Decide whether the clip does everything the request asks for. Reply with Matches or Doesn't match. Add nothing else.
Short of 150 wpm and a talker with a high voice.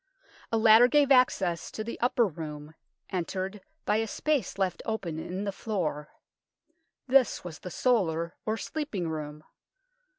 Matches